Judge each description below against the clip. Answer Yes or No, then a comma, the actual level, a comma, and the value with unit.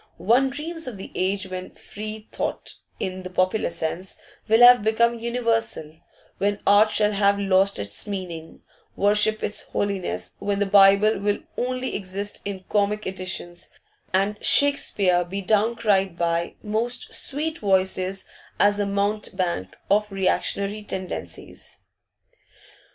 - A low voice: No, high, 200 Hz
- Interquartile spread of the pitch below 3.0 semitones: Yes, narrow, 2.4 semitones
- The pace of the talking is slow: Yes, slow, 130 wpm